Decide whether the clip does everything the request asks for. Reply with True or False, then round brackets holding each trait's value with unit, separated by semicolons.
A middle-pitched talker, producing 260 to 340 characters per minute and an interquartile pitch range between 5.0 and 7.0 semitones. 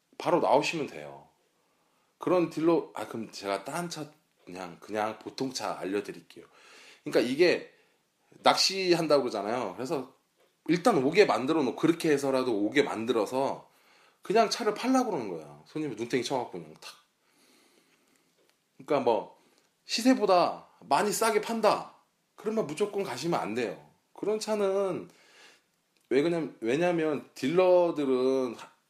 False (175 Hz; 295 characters per minute; 7.8 semitones)